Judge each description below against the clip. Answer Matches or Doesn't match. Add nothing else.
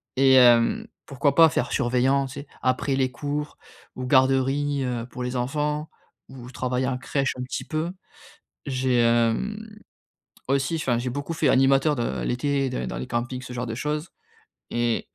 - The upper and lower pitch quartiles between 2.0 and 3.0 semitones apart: Matches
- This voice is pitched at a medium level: Doesn't match